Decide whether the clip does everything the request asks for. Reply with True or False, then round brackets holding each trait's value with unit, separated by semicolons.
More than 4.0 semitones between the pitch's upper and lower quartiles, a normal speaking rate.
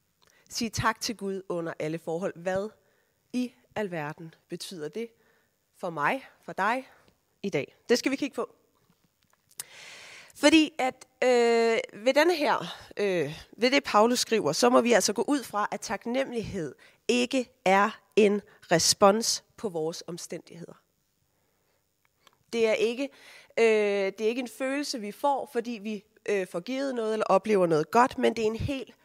True (4.5 semitones; 155 wpm)